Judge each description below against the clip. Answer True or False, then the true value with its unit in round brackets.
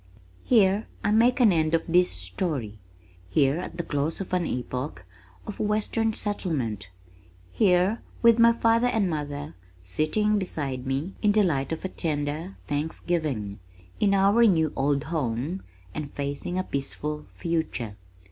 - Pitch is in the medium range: True (160 Hz)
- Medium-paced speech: True (145 wpm)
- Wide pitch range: True (5.9 semitones)